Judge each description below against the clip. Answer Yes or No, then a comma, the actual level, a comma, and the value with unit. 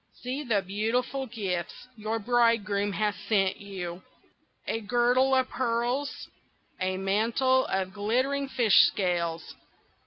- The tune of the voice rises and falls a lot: No, average, 4.3 semitones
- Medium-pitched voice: No, high, 220 Hz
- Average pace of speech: No, slow, 115 wpm